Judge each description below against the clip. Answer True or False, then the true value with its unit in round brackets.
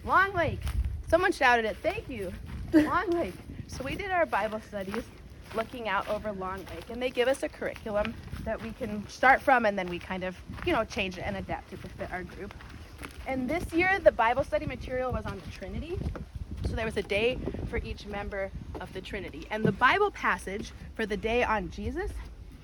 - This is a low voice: False (235 Hz)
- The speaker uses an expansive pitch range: True (6.5 semitones)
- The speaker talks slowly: False (205 wpm)